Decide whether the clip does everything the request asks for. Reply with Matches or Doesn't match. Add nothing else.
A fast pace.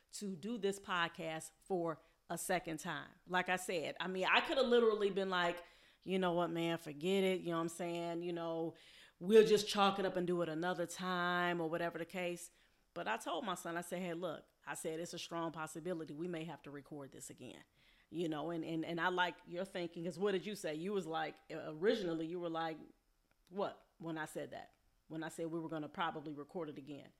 Matches